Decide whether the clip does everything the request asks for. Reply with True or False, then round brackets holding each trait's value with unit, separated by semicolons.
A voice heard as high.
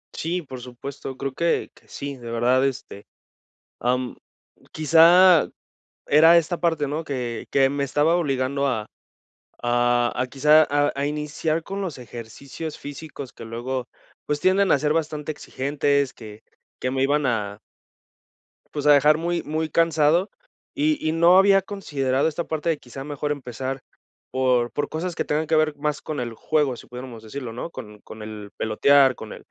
False (140 Hz)